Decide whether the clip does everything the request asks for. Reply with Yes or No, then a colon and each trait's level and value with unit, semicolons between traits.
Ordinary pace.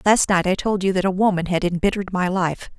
No: fast, 260 wpm